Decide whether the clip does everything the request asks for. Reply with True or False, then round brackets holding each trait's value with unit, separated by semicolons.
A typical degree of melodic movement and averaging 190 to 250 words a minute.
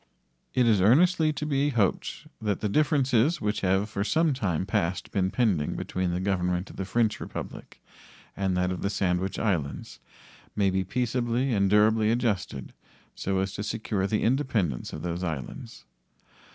False (4.3 semitones; 165 wpm)